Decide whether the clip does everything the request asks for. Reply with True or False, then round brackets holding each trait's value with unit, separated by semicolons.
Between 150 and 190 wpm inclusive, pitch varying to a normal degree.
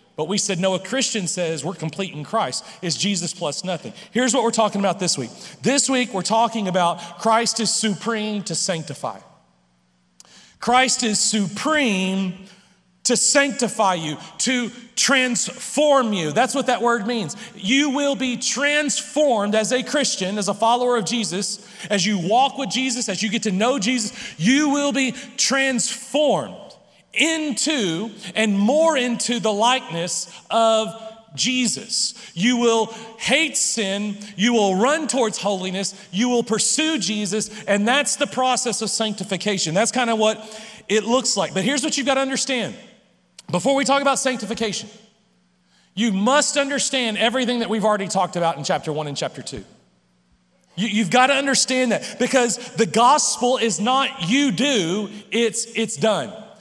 True (160 wpm; 4.5 semitones)